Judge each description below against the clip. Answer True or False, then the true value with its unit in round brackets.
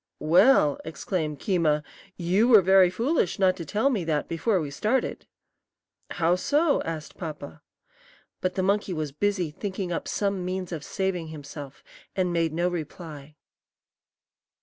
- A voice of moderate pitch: True (180 Hz)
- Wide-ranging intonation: False (3.7 semitones)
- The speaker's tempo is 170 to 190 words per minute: False (145 wpm)